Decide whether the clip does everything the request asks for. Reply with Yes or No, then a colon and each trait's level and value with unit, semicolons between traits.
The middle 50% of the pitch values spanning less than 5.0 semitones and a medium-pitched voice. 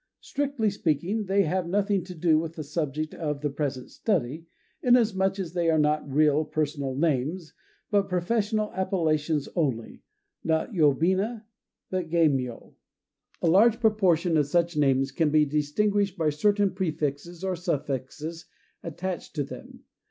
Yes: average, 4.3 semitones; medium, 165 Hz